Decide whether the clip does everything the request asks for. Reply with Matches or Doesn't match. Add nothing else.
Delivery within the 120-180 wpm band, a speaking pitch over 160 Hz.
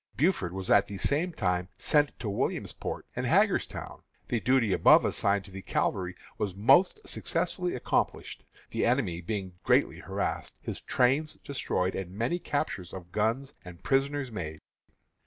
Doesn't match